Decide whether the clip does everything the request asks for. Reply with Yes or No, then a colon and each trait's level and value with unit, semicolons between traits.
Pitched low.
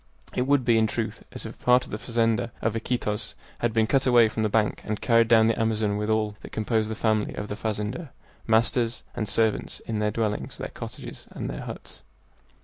Yes: low, 110 Hz